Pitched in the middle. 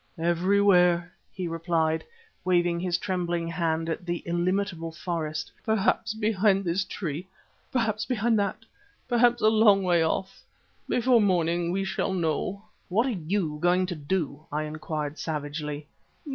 Yes: medium, 175 Hz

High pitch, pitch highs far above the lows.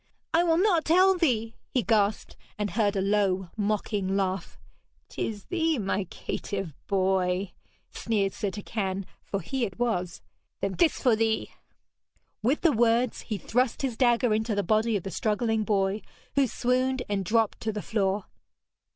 No: high, 215 Hz; average, 3.7 semitones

